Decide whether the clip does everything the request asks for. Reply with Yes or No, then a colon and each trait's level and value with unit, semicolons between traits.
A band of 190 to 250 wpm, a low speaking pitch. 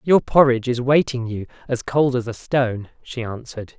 No: average, 175 wpm; low, 125 Hz